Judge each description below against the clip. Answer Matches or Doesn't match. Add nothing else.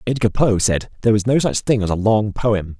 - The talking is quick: Matches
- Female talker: Doesn't match